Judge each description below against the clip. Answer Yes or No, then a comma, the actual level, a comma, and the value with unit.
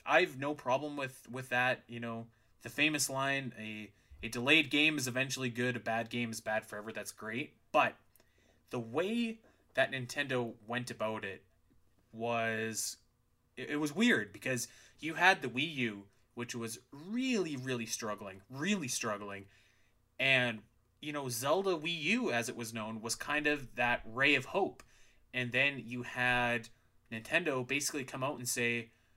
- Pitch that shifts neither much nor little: Yes, average, 3.3 semitones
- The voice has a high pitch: No, low, 120 Hz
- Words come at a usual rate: Yes, average, 160 wpm